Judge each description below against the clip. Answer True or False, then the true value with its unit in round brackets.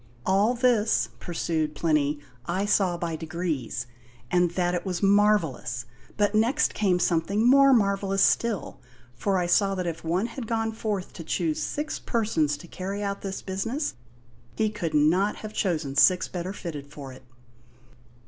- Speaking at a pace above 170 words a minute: False (160 wpm)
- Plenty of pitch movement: False (4.2 semitones)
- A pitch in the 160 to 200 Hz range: True (185 Hz)